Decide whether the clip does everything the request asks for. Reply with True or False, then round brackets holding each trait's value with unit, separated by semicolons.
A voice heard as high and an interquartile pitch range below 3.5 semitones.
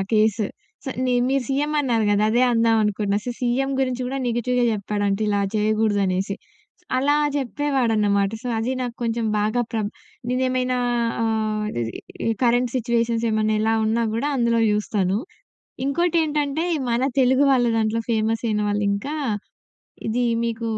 True (230 Hz; 2.9 semitones)